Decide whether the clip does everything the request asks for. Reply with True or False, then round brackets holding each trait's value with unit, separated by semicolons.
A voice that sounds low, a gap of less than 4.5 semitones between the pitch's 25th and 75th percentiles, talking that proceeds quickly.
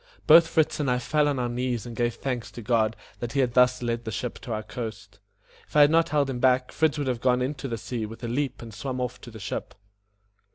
True (125 Hz; 2.7 semitones; 260 wpm)